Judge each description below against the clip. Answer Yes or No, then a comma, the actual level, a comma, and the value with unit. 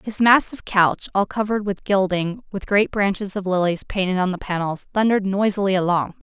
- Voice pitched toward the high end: Yes, high, 195 Hz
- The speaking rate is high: No, average, 180 wpm